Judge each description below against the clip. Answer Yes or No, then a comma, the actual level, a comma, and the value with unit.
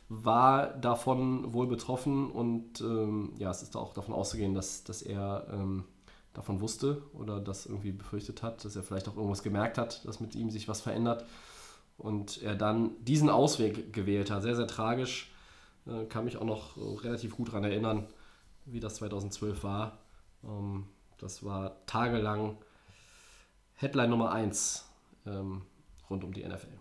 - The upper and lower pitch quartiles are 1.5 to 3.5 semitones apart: Yes, average, 2.8 semitones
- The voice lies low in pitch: Yes, low, 110 Hz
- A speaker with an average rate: Yes, average, 160 wpm